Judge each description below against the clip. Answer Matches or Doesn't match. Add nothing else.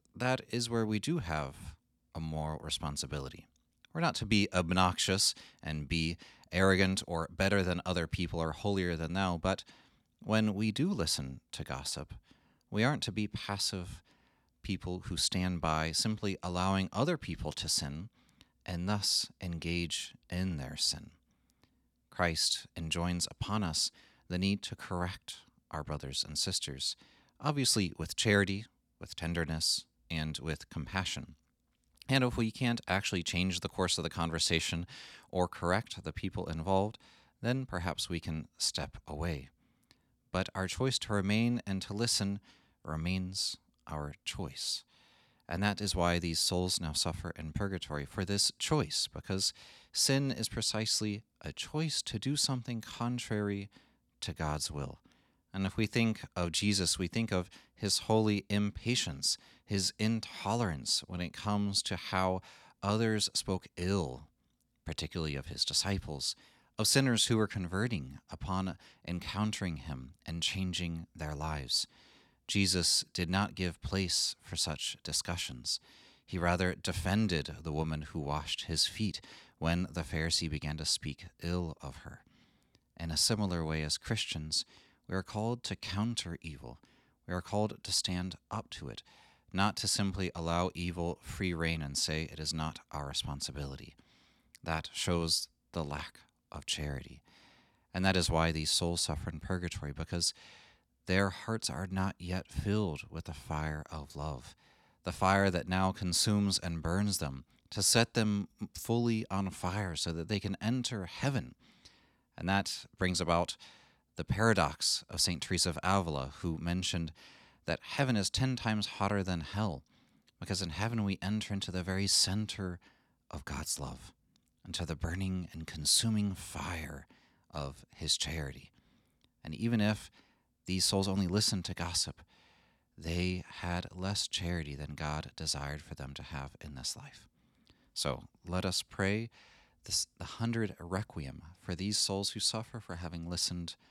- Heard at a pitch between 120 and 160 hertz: Doesn't match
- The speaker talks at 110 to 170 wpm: Matches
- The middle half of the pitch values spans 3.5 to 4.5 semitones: Matches